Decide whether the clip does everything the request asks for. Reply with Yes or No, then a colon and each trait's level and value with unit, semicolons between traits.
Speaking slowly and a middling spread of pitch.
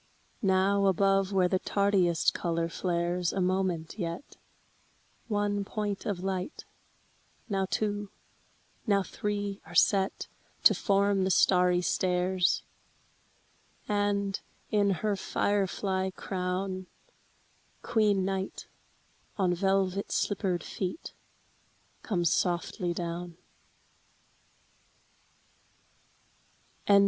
No: slow, 90 wpm; narrow, 1.9 semitones